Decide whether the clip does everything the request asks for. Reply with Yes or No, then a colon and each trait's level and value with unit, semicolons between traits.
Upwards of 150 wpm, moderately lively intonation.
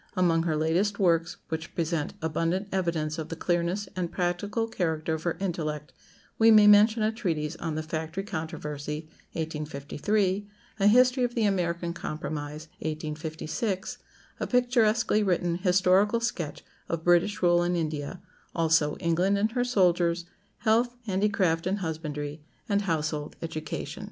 No: average, 140 wpm; average, 4.2 semitones